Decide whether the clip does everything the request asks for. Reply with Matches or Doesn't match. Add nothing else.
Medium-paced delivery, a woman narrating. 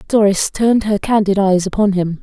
Matches